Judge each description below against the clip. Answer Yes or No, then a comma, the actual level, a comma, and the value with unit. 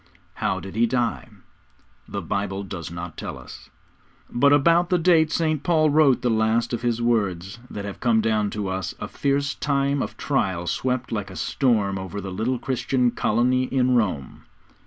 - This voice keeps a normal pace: Yes, average, 180 wpm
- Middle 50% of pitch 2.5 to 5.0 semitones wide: No, wide, 5.5 semitones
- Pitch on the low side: Yes, low, 120 Hz